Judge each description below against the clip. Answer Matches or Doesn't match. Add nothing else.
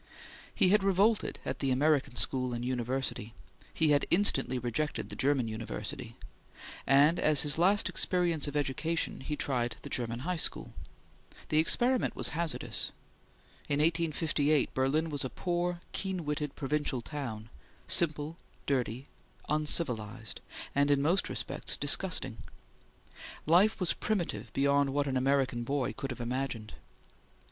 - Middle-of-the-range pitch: Matches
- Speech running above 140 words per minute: Doesn't match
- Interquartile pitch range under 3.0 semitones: Doesn't match